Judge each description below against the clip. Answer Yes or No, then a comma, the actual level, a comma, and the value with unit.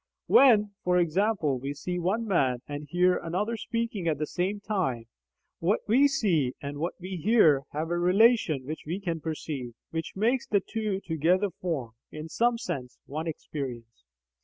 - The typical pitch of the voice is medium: Yes, medium, 175 Hz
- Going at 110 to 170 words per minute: Yes, average, 165 wpm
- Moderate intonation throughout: No, wide, 5.9 semitones